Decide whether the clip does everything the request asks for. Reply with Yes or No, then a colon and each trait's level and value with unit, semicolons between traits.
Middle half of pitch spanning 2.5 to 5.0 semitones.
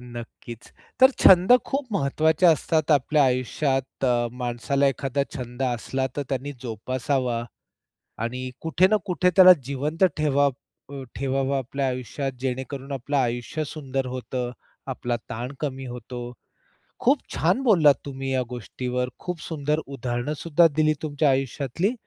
Yes: average, 3.3 semitones